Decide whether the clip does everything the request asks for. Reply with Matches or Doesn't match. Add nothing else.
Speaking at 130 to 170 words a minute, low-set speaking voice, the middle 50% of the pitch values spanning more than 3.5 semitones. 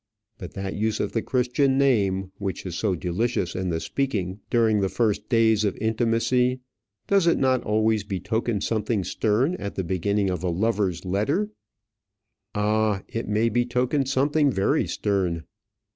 Matches